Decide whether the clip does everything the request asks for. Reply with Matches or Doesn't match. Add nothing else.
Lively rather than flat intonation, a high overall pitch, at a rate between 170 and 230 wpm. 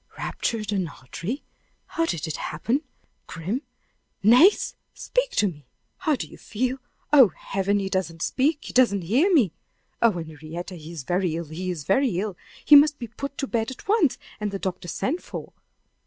Matches